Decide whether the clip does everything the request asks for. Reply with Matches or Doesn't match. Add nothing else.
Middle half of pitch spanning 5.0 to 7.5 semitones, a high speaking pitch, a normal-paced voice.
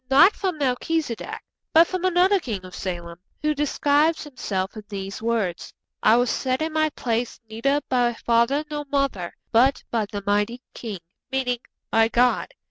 Matches